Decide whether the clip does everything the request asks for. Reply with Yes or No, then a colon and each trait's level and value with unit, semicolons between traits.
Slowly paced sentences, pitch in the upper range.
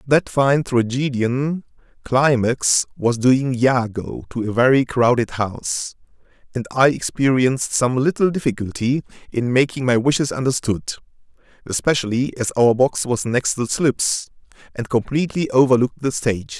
No: slow, 130 wpm; low, 125 Hz